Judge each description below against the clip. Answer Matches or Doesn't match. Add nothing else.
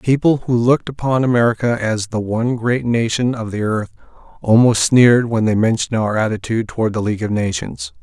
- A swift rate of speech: Doesn't match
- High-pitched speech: Doesn't match